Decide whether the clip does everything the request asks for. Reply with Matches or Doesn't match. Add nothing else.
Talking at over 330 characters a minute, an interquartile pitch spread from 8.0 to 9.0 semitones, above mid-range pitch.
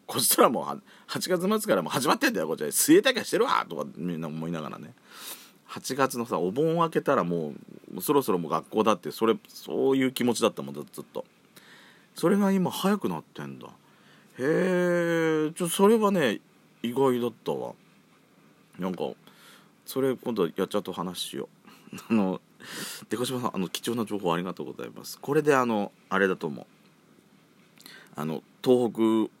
Doesn't match